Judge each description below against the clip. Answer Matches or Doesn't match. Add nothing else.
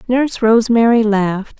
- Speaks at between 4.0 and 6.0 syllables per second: Matches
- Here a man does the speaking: Doesn't match